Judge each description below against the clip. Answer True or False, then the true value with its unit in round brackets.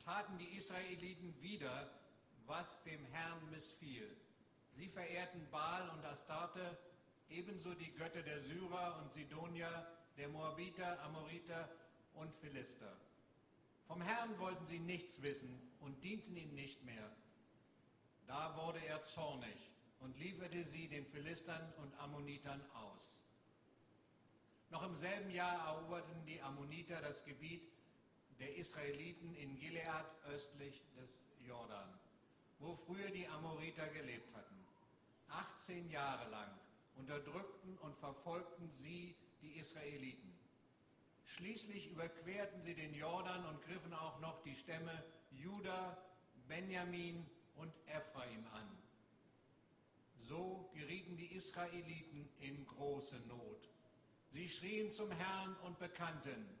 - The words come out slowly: True (115 wpm)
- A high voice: False (165 Hz)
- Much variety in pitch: False (3.6 semitones)